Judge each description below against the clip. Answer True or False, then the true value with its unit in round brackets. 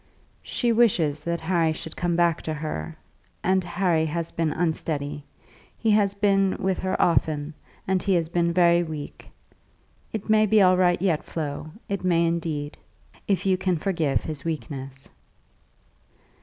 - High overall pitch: False (170 Hz)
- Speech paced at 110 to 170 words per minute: True (155 wpm)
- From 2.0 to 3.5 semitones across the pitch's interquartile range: True (3.2 semitones)